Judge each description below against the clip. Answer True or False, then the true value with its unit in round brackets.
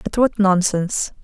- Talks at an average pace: True (145 wpm)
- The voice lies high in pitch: True (200 Hz)